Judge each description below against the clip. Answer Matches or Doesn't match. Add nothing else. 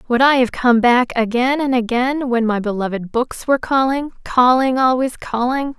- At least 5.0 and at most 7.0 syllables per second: Doesn't match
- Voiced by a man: Doesn't match